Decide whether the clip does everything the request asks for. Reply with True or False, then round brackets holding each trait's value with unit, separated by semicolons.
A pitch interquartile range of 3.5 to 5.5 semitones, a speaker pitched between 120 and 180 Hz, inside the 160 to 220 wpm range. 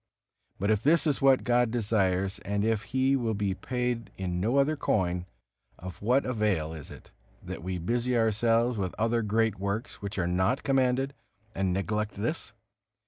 False (4.3 semitones; 110 Hz; 170 wpm)